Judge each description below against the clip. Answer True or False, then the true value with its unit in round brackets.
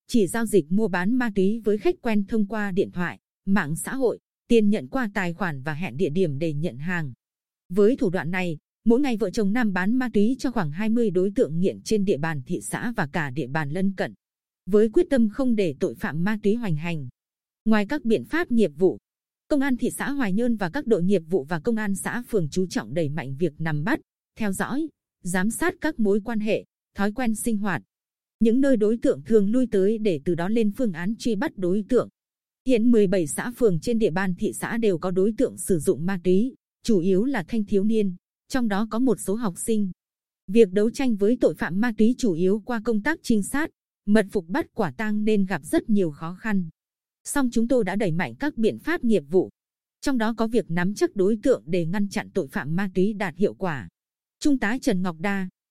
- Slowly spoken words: False (235 wpm)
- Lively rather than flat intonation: False (3.9 semitones)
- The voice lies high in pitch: True (210 Hz)